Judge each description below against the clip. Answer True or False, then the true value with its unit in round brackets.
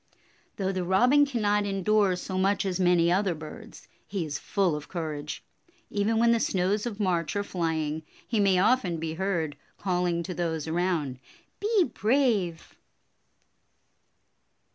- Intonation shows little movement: False (3.7 semitones)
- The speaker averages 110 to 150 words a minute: True (140 wpm)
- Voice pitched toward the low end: False (185 Hz)